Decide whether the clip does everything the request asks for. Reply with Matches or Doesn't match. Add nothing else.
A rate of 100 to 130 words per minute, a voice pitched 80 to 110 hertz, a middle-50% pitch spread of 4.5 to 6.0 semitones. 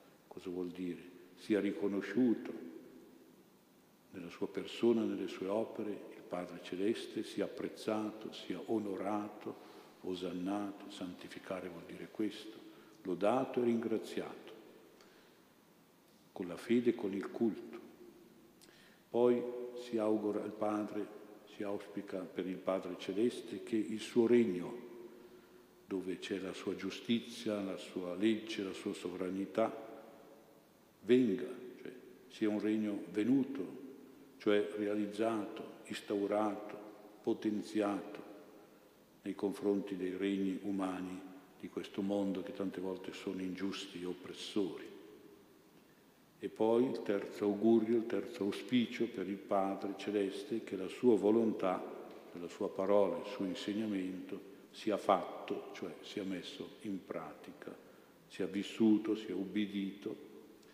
Doesn't match